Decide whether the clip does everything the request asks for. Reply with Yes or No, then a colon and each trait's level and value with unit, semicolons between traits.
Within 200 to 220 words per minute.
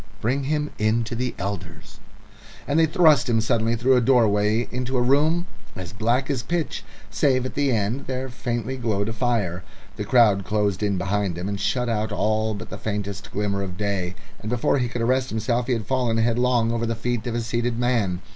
Yes: fast, 205 wpm